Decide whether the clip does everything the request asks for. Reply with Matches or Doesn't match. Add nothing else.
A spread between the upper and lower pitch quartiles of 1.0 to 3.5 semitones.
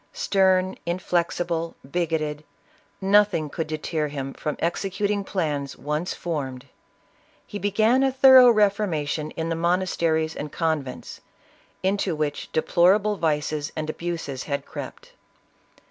Doesn't match